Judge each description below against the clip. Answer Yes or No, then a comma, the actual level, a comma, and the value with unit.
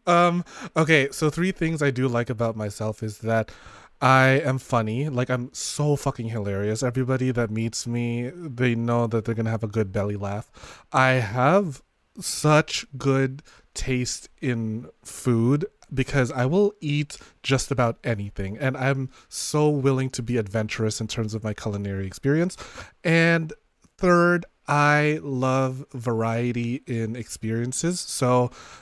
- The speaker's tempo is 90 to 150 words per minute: Yes, average, 145 wpm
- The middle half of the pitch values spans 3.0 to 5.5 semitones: Yes, average, 4.2 semitones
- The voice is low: Yes, low, 130 Hz